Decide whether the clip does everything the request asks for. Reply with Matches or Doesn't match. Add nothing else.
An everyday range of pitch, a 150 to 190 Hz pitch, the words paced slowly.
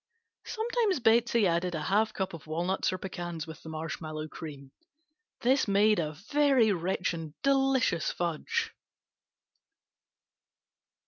Doesn't match